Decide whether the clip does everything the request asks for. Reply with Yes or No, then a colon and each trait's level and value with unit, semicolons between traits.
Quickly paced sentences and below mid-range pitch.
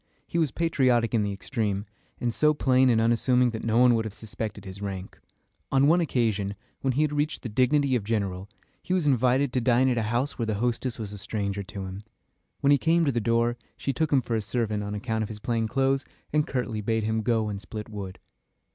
Yes: fast, 230 wpm; low, 115 Hz